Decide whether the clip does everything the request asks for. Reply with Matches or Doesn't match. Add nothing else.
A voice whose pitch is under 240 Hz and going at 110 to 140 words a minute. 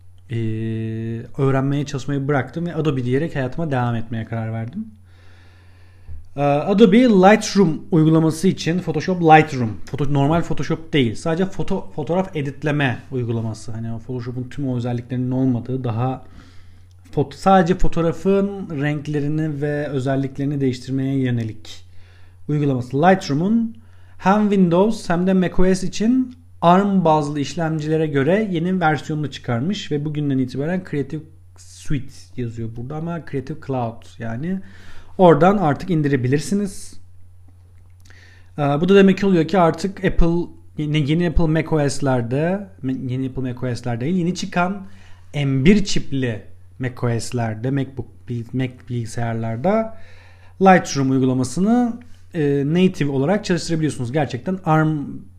Matches